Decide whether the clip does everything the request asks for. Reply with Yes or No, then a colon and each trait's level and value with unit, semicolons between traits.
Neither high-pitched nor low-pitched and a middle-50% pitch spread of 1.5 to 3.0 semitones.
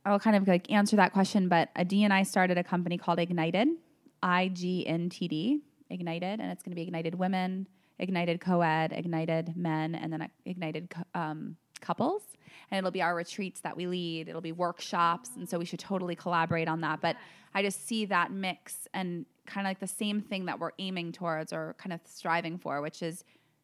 Yes: medium, 175 Hz; narrow, 2.5 semitones